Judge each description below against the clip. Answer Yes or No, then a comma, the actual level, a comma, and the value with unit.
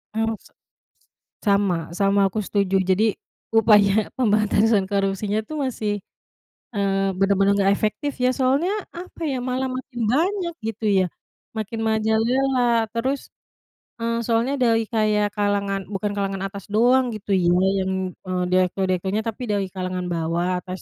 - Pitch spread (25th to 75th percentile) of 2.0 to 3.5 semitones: Yes, average, 2.9 semitones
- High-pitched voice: Yes, high, 210 Hz